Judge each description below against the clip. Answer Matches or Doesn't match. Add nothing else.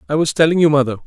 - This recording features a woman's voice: Doesn't match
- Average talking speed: Doesn't match